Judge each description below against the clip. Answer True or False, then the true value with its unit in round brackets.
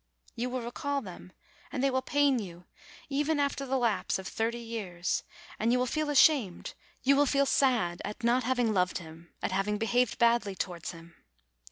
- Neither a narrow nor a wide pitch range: False (5.9 semitones)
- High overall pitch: True (235 Hz)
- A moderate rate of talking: True (190 wpm)